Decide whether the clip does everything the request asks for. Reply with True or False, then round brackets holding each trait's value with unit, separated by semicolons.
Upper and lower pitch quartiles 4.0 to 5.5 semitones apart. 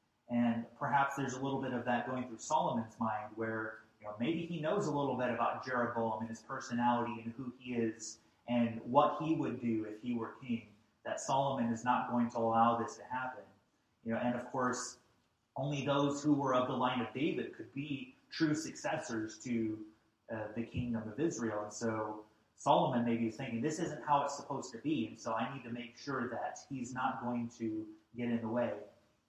False (2.9 semitones)